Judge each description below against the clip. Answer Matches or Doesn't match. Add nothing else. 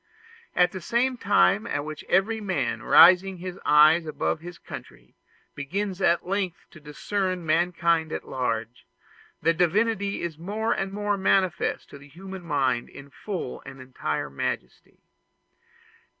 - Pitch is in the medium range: Matches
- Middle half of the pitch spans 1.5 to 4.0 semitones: Doesn't match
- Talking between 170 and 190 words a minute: Doesn't match